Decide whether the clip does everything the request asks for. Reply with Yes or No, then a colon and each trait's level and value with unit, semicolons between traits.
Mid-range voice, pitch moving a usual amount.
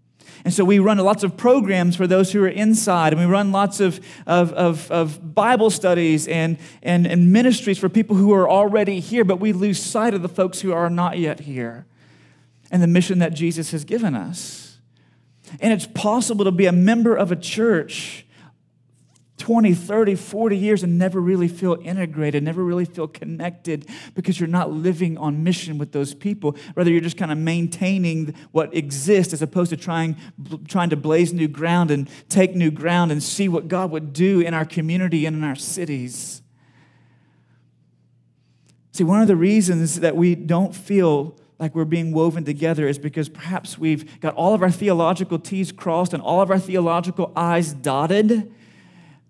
Yes: medium, 175 Hz; average, 3.2 semitones